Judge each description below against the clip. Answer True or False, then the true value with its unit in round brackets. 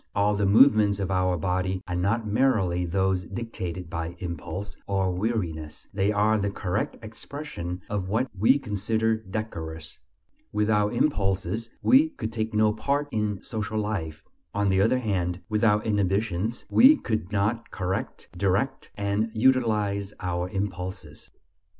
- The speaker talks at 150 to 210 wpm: False (140 wpm)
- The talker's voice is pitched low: True (100 Hz)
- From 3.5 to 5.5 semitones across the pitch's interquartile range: False (3.0 semitones)